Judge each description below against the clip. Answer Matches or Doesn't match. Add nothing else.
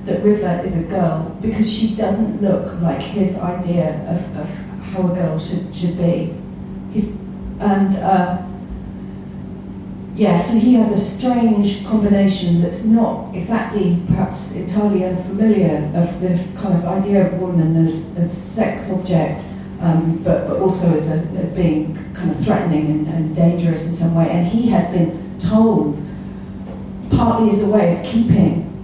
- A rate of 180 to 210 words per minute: Doesn't match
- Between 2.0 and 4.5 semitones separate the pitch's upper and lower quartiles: Matches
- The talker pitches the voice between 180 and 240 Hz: Matches